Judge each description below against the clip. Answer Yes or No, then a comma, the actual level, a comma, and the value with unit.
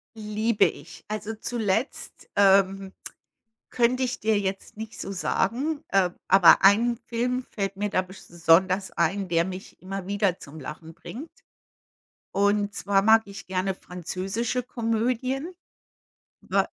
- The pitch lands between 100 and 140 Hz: No, high, 200 Hz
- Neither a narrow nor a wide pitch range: Yes, average, 3.3 semitones